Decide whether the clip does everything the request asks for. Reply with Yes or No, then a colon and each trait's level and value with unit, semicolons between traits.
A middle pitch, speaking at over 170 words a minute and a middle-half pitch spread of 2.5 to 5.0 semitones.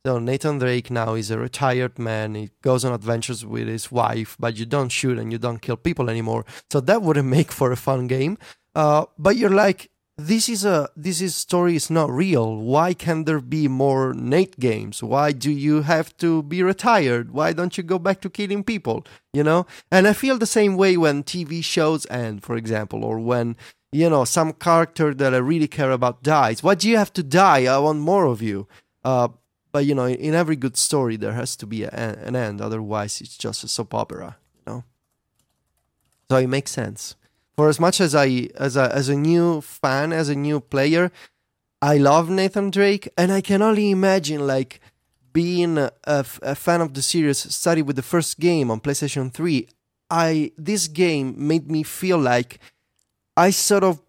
No: medium, 145 Hz; average, 200 wpm; wide, 5.4 semitones